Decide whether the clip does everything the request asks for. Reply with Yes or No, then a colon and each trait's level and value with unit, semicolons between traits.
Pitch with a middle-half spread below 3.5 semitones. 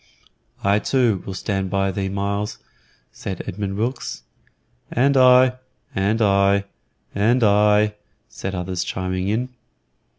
Yes: narrow, 2.6 semitones